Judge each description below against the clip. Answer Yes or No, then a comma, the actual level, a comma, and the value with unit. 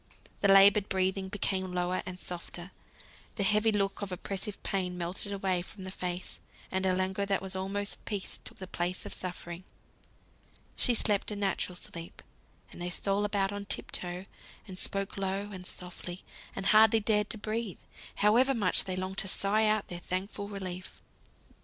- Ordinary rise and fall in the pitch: No, narrow, 1.8 semitones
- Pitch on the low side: No, high, 195 Hz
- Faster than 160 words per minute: Yes, average, 170 wpm